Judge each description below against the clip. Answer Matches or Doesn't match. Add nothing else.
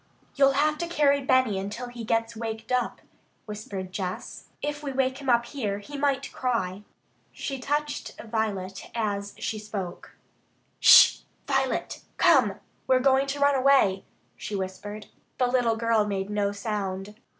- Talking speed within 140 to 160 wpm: Matches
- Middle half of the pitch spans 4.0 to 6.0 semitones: Matches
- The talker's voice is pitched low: Doesn't match